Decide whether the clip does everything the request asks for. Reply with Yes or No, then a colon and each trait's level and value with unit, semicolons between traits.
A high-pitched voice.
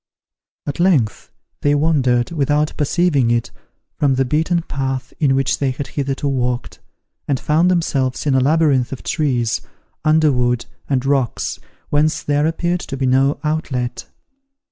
No: medium, 140 Hz